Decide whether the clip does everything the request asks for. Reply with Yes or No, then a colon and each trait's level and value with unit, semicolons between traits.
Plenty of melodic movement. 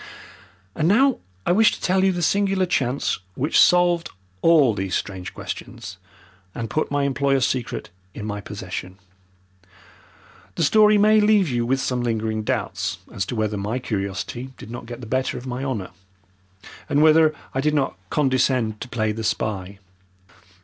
Yes: wide, 6.9 semitones